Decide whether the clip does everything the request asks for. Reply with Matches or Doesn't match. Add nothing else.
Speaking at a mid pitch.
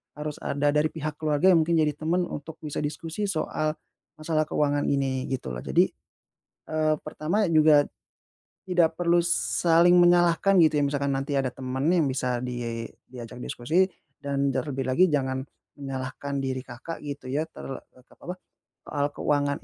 Matches